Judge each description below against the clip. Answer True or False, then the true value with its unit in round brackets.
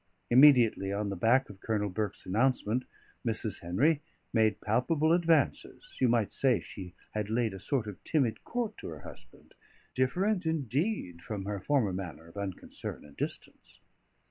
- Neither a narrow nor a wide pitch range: False (5.8 semitones)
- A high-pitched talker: False (110 Hz)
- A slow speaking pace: False (155 wpm)